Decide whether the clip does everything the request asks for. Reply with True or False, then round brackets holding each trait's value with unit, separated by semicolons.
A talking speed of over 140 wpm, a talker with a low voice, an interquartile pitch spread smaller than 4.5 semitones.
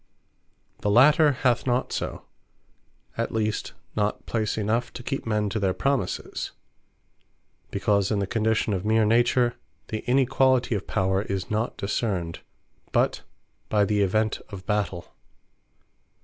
False (135 wpm; 110 Hz; 3.0 semitones)